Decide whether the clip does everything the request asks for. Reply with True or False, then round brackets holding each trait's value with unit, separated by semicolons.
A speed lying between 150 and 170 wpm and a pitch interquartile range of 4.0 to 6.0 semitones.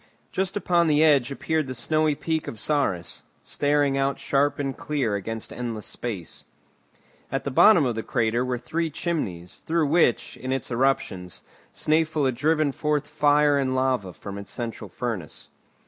True (165 wpm; 4.5 semitones)